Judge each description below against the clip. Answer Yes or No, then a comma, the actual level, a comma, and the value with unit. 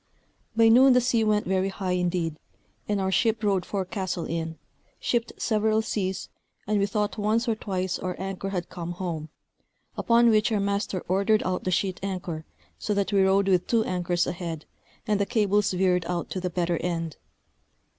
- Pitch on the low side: No, high, 190 Hz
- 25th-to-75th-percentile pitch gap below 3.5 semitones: Yes, average, 2.9 semitones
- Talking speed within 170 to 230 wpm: Yes, average, 180 wpm